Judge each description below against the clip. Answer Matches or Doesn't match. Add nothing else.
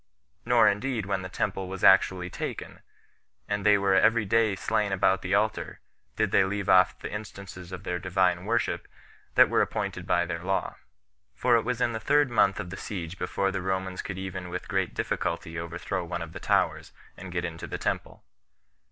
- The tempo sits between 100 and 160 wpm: Doesn't match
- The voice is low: Matches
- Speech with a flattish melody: Matches